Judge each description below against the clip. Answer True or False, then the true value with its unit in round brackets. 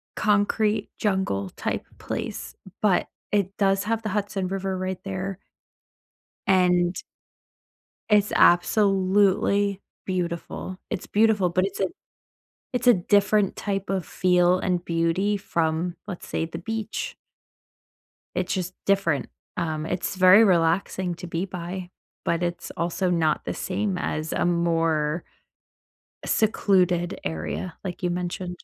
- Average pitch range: False (2.3 semitones)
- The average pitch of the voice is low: False (185 Hz)